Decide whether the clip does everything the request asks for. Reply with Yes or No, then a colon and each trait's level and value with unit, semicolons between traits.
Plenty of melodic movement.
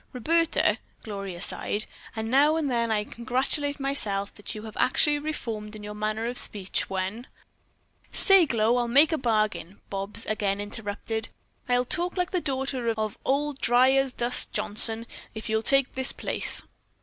No: average, 4.3 semitones